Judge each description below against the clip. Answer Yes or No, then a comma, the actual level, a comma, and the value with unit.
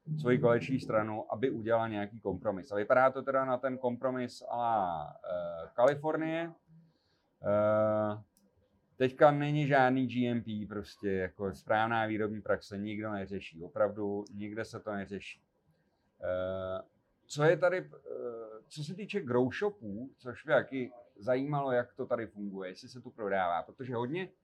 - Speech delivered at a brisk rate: No, average, 140 wpm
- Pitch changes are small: No, average, 4.4 semitones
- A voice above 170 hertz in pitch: No, low, 120 Hz